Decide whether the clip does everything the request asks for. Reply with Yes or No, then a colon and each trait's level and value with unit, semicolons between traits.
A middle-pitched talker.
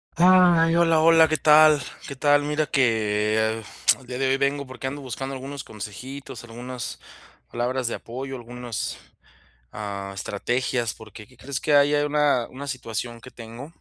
No: low, 130 Hz